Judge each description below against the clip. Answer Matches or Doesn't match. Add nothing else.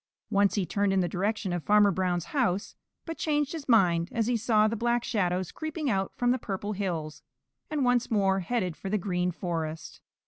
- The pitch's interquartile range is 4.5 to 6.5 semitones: Matches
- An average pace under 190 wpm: Doesn't match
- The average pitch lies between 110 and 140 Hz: Doesn't match